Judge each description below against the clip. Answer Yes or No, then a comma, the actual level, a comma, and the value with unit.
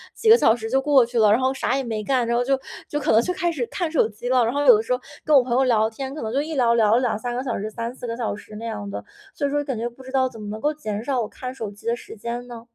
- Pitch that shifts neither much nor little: Yes, average, 3.1 semitones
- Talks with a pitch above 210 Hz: Yes, high, 245 Hz